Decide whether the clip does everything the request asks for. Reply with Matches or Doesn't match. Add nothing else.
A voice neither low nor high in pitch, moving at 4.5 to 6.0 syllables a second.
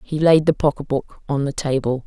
Matches